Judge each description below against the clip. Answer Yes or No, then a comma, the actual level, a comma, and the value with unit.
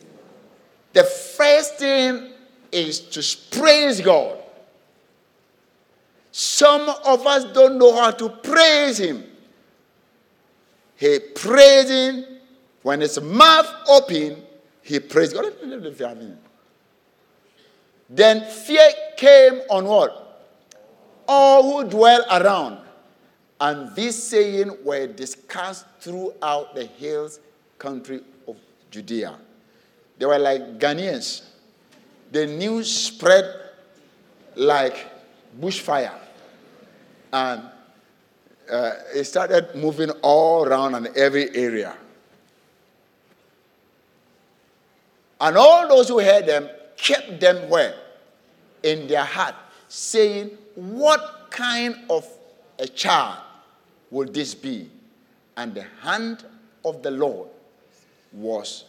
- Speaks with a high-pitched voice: Yes, high, 220 Hz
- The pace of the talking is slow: Yes, slow, 95 wpm